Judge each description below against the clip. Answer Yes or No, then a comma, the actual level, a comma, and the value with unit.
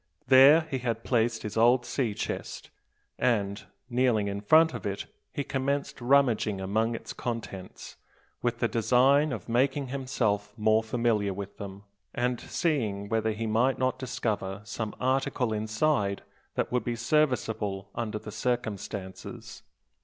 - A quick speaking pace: No, average, 140 wpm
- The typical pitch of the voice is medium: No, low, 115 Hz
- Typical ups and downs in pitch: Yes, average, 3.7 semitones